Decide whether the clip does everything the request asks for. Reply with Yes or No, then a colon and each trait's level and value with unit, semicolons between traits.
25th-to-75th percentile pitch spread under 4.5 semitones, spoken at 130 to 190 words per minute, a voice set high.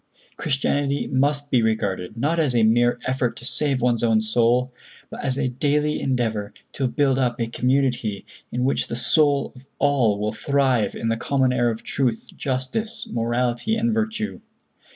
No: average, 3.2 semitones; average, 170 wpm; low, 125 Hz